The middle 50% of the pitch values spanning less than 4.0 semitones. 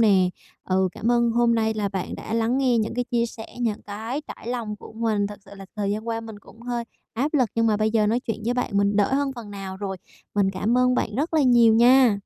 Yes: average, 2.7 semitones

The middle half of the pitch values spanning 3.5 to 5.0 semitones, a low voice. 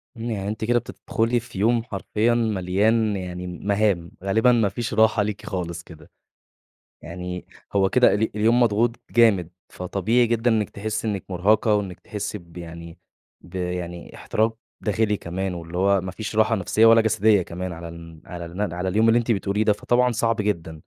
Yes: average, 3.8 semitones; low, 105 Hz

